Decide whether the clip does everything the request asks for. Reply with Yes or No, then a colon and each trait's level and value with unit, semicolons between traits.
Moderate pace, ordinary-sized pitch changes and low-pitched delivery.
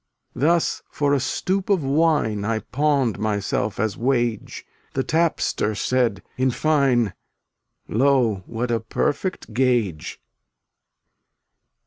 No: slow, 115 wpm; average, 4.7 semitones; low, 125 Hz